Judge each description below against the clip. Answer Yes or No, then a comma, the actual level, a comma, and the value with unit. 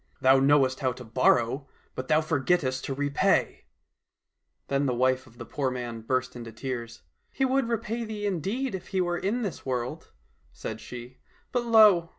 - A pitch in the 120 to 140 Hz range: Yes, low, 135 Hz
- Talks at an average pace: Yes, average, 190 wpm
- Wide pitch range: Yes, wide, 6.9 semitones